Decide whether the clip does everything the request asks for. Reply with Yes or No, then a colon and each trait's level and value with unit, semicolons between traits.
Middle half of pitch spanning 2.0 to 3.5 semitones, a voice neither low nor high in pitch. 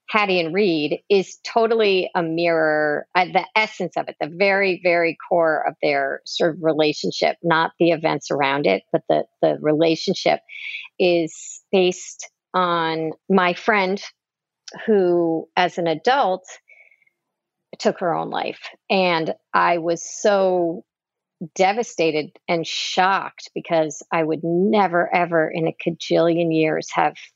Yes: average, 2.9 semitones; medium, 175 Hz